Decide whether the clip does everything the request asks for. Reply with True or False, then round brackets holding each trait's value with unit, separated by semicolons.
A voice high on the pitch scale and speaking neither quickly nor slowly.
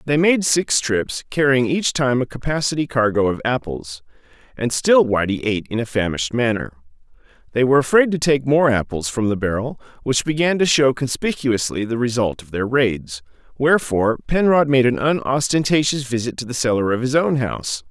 False (125 Hz; 180 wpm)